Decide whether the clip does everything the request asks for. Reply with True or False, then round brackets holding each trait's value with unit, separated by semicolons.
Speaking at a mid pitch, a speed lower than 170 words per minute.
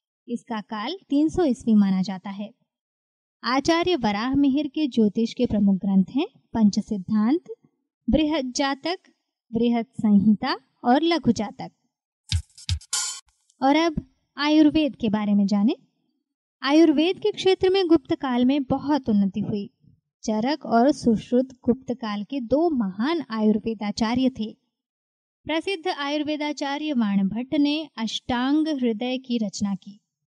False (255 Hz; 120 wpm)